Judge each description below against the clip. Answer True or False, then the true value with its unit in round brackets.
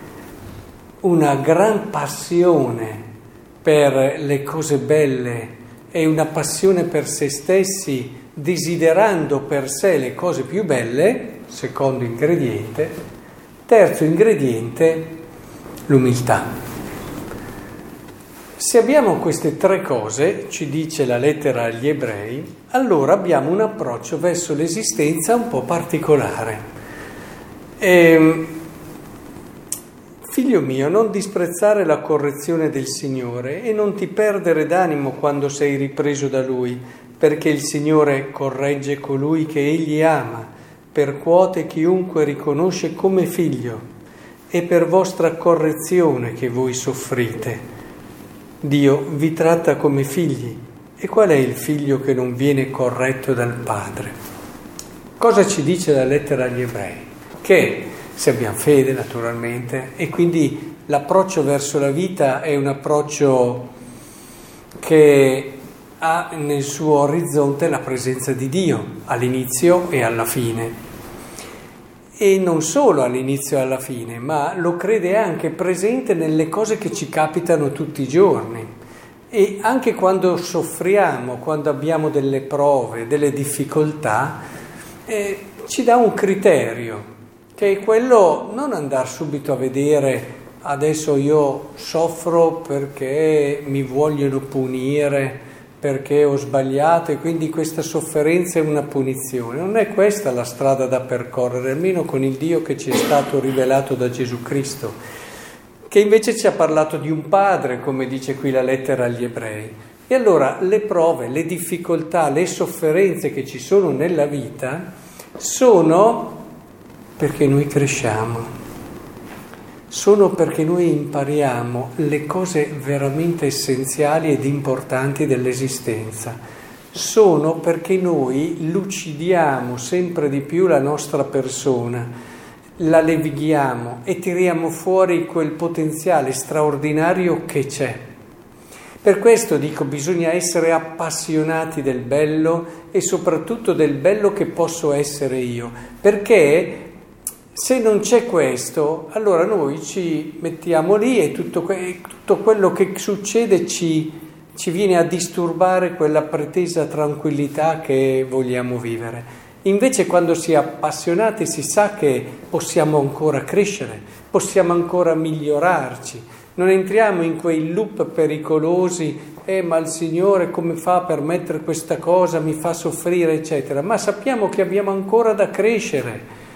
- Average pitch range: True (4.3 semitones)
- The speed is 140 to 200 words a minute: False (125 wpm)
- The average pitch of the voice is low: False (155 Hz)